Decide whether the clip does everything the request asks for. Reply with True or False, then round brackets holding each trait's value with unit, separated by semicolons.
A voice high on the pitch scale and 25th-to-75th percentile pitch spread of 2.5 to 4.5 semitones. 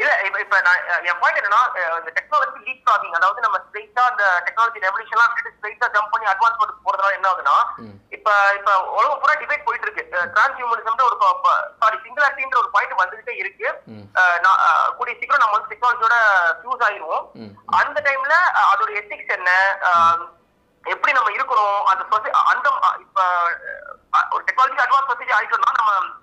False (220 Hz; 5.2 semitones)